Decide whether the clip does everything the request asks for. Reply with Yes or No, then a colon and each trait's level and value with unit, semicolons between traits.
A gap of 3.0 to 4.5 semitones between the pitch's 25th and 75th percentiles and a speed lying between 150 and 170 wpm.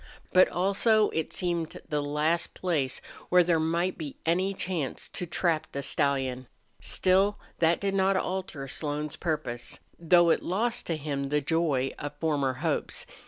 Yes: average, 3.9 semitones; average, 155 wpm